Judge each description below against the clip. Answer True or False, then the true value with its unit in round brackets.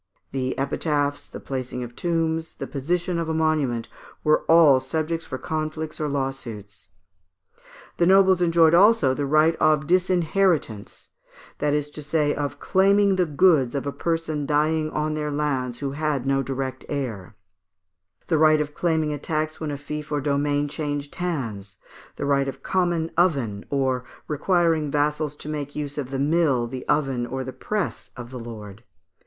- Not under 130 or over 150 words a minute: False (165 wpm)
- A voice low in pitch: False (150 Hz)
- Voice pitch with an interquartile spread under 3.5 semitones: True (3.1 semitones)